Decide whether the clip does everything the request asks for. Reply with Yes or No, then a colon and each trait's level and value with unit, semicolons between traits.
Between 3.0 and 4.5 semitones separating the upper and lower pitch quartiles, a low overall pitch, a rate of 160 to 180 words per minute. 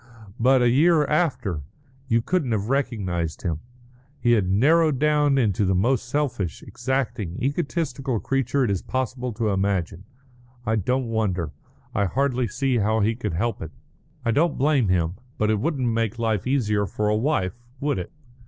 No: average, 5.1 semitones; low, 115 Hz; average, 165 wpm